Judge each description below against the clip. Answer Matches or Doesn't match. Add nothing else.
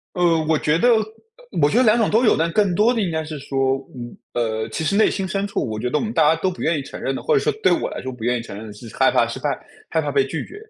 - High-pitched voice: Doesn't match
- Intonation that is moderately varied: Doesn't match